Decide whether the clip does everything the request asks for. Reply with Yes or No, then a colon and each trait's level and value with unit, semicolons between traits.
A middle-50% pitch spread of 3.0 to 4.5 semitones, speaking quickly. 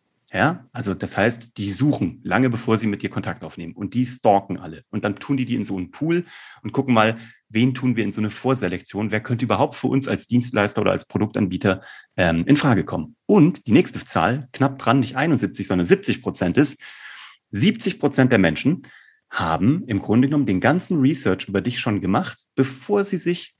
No: average, 5.1 semitones; fast, 205 wpm